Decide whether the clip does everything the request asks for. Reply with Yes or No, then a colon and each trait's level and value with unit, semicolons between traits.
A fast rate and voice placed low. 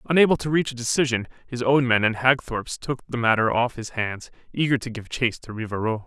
Yes: fast, 220 wpm; low, 120 Hz